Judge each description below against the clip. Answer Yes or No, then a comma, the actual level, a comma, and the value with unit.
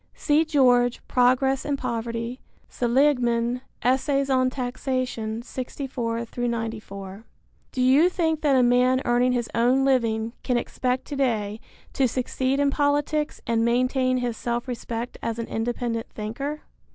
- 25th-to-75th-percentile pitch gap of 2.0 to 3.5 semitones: Yes, narrow, 2.4 semitones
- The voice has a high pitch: Yes, very high, 250 Hz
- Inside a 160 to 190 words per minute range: No, slow, 135 wpm